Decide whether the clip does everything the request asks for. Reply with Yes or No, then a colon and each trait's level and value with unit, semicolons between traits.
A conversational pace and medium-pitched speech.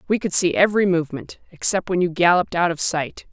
No: fast, 215 wpm; medium, 175 Hz